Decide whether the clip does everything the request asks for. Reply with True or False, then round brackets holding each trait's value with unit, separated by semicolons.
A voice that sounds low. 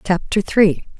False (190 Hz)